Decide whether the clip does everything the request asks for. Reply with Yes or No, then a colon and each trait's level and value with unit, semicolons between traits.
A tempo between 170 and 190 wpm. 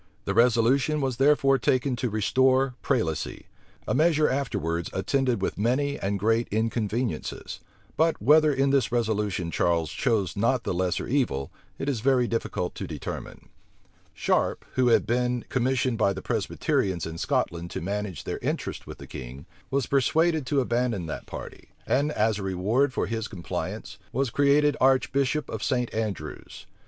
No: average, 155 wpm